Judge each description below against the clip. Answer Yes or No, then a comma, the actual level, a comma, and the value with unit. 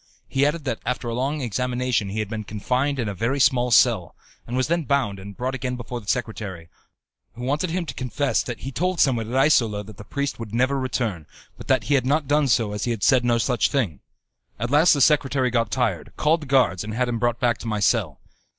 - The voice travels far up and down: No, average, 3.7 semitones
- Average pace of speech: No, fast, 240 wpm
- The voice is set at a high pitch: No, low, 125 Hz